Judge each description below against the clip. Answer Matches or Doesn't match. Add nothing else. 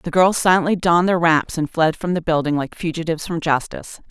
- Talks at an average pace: Doesn't match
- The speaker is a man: Doesn't match